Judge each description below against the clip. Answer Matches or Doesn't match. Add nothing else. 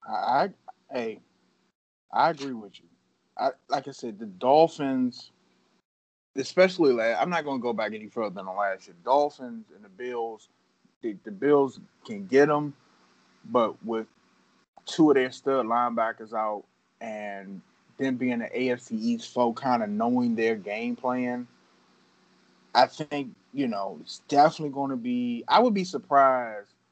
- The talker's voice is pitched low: Matches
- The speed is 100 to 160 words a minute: Matches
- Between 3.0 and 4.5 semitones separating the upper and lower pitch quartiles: Doesn't match